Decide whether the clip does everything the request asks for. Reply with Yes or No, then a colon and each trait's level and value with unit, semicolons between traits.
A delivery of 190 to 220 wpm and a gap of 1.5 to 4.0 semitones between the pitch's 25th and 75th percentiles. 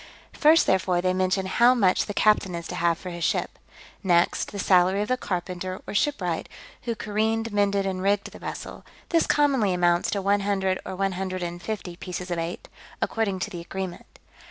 Yes: average, 195 wpm; narrow, 2.5 semitones